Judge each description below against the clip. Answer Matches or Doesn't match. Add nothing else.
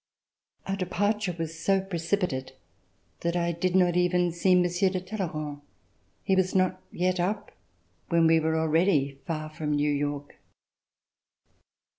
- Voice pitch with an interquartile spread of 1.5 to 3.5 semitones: Matches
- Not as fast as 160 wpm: Matches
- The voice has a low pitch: Doesn't match